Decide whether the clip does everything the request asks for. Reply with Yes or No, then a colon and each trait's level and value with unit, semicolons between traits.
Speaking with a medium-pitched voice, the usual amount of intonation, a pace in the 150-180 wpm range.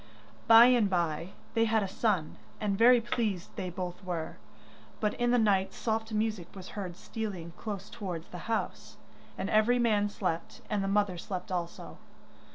No: high, 205 Hz; average, 3.6 semitones; average, 165 wpm